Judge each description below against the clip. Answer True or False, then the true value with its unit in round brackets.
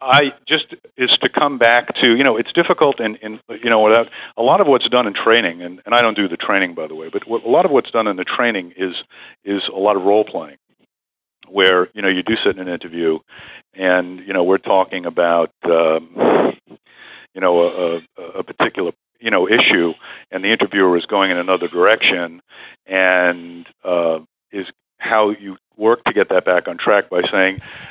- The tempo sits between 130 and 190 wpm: False (205 wpm)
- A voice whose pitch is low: True (95 Hz)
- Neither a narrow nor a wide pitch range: True (3.5 semitones)